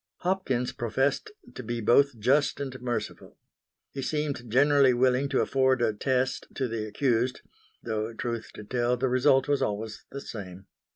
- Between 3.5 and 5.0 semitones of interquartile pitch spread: No, average, 2.9 semitones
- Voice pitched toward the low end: Yes, low, 125 Hz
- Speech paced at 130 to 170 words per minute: Yes, average, 160 wpm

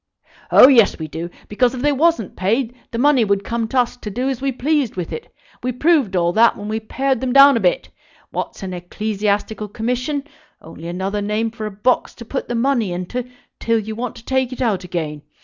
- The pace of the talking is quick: Yes, fast, 220 wpm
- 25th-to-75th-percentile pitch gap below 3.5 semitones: No, average, 4.4 semitones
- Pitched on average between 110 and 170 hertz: No, high, 230 Hz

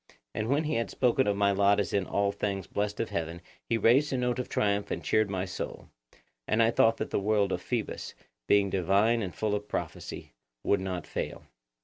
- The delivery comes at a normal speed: No, fast, 215 wpm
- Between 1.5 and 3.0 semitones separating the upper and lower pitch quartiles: Yes, narrow, 2.6 semitones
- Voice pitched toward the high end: No, low, 100 Hz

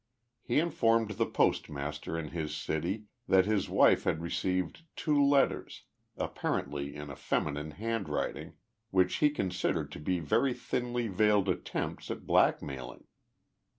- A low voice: Yes, very low, 95 Hz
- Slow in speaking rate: Yes, slow, 130 wpm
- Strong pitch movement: Yes, wide, 6.9 semitones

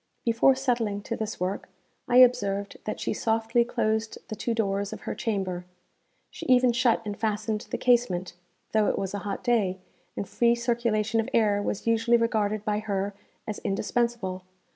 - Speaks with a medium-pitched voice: No, high, 220 Hz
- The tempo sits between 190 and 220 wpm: No, average, 170 wpm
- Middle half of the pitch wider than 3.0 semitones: No, average, 2.7 semitones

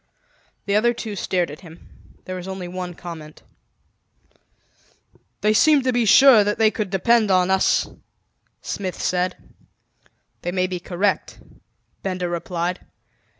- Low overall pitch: No, medium, 185 Hz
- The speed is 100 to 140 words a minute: Yes, slow, 135 wpm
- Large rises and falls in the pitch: No, average, 3.0 semitones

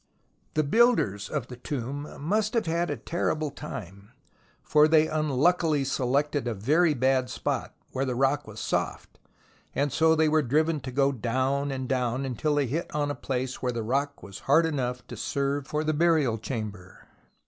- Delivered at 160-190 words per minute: Yes, average, 180 wpm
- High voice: No, medium, 140 Hz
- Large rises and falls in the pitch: No, average, 3.5 semitones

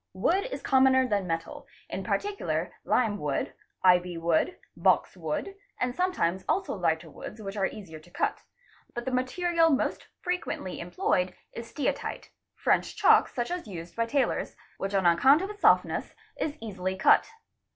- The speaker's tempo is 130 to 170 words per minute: Yes, average, 160 wpm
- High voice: Yes, high, 215 Hz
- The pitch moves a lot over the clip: Yes, wide, 8.3 semitones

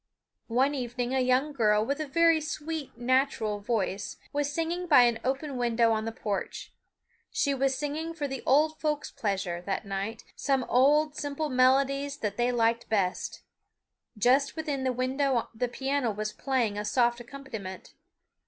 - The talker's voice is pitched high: Yes, very high, 255 Hz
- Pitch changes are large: No, average, 4.0 semitones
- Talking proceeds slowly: No, average, 160 wpm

